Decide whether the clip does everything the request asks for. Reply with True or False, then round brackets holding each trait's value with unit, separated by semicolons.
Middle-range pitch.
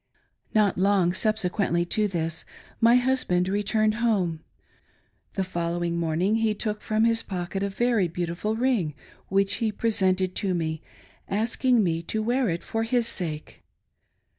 False (200 Hz)